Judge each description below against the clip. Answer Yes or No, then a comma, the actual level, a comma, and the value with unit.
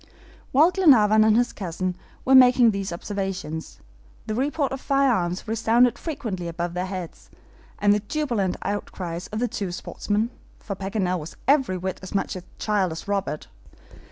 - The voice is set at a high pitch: Yes, high, 205 Hz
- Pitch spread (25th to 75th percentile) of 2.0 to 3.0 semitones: No, average, 4.8 semitones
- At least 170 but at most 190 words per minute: No, average, 155 wpm